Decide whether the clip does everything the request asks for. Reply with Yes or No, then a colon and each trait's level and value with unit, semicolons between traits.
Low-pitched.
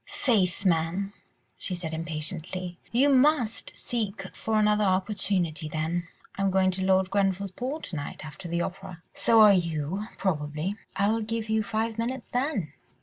No: high, 190 Hz